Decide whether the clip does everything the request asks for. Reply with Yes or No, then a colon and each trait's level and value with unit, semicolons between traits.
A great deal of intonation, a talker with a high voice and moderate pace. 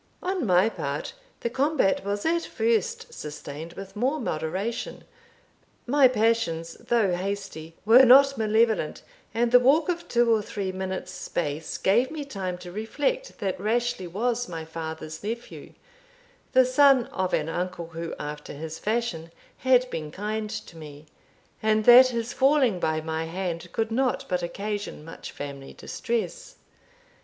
Yes: wide, 6.6 semitones; high, 210 Hz; average, 150 wpm